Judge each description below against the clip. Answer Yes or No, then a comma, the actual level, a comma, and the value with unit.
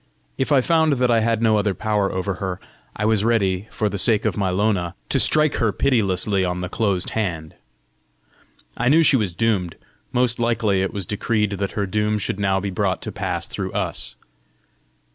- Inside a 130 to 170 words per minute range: No, average, 195 wpm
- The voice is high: No, low, 105 Hz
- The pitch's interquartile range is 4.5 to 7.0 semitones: No, average, 3.2 semitones